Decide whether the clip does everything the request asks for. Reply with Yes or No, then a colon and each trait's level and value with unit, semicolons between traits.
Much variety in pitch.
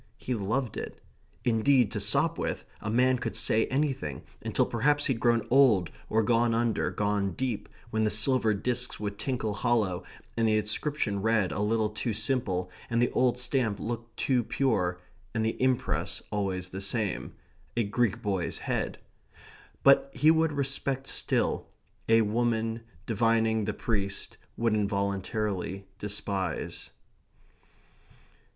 No: average, 3.3 semitones